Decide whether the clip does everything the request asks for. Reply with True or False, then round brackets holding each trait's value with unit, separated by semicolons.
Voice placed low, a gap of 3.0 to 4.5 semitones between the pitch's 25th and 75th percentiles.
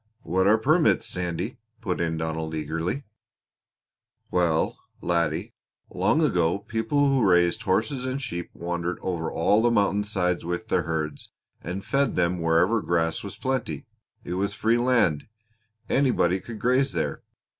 False (90 Hz; 5.3 semitones)